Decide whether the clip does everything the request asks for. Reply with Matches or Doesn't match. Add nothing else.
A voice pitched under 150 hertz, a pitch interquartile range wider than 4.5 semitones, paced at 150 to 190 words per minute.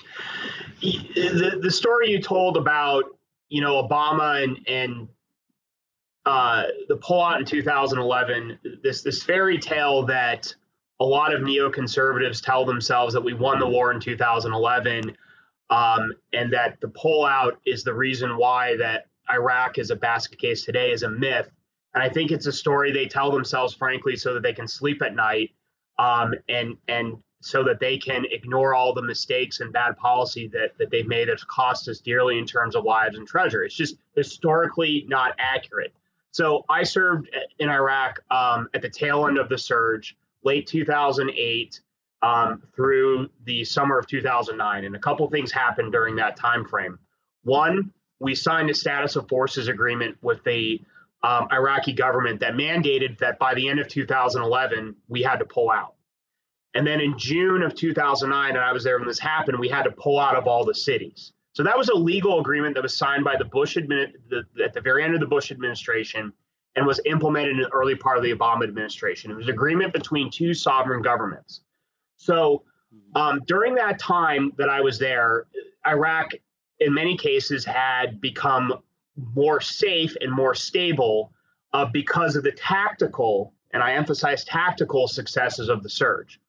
Doesn't match